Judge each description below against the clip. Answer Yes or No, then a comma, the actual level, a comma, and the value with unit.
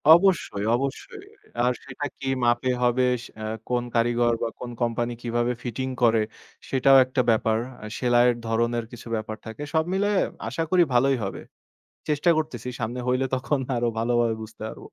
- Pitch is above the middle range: No, low, 120 Hz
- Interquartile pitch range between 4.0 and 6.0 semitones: No, narrow, 2.5 semitones